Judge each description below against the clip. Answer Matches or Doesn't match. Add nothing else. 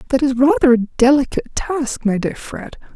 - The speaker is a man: Doesn't match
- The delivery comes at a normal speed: Matches